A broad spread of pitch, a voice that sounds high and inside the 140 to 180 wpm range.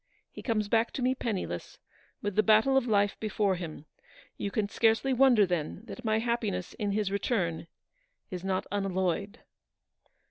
No: average, 3.0 semitones; high, 210 Hz; average, 155 wpm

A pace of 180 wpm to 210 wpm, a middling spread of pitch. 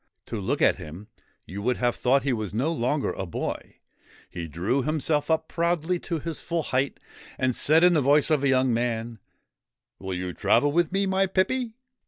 No: average, 200 wpm; wide, 6.2 semitones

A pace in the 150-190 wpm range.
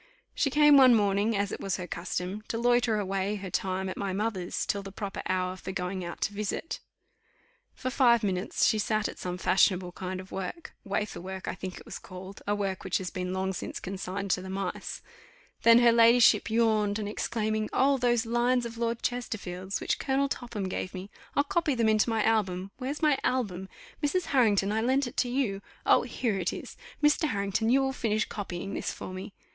No: fast, 205 wpm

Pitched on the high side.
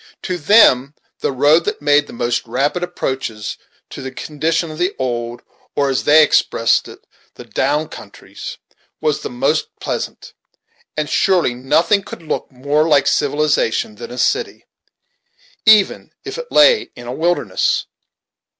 No: medium, 145 Hz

